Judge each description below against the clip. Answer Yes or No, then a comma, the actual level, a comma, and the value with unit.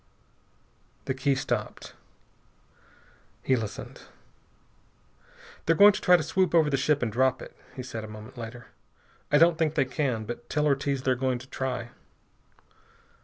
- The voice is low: Yes, low, 130 Hz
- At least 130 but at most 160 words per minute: Yes, average, 155 wpm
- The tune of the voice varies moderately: Yes, average, 3.7 semitones